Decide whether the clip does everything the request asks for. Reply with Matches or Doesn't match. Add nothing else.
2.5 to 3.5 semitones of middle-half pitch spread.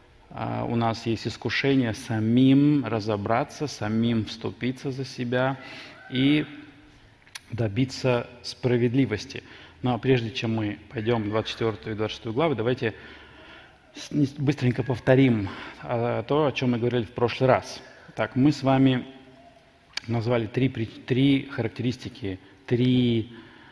Matches